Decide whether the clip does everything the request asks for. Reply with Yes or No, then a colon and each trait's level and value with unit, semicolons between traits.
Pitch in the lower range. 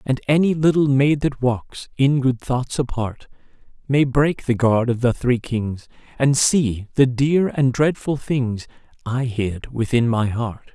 Yes: low, 130 Hz